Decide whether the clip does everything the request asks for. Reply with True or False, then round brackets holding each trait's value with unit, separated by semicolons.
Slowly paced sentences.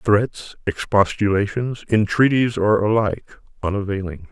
True (85 wpm)